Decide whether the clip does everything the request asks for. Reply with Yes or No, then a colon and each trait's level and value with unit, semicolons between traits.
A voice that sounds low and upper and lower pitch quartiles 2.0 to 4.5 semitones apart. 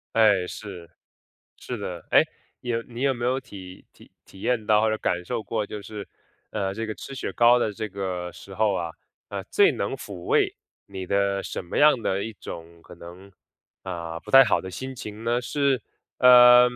Yes: low, 105 Hz; average, 4.1 semitones